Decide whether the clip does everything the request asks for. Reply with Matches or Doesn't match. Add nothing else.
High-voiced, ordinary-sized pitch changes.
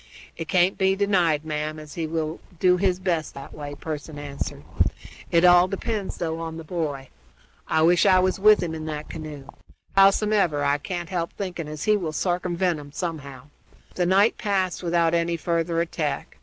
Doesn't match